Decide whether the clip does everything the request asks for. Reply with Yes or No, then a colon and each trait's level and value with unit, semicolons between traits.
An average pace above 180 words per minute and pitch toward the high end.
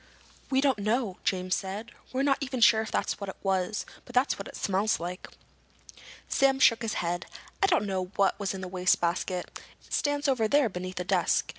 Yes: average, 200 wpm; high, 205 Hz